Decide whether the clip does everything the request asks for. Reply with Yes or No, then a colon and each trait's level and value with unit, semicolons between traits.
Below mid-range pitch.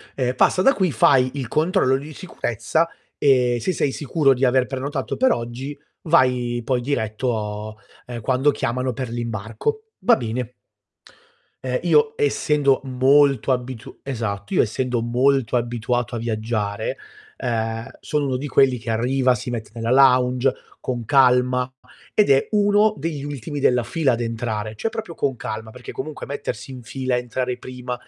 Yes: low, 125 Hz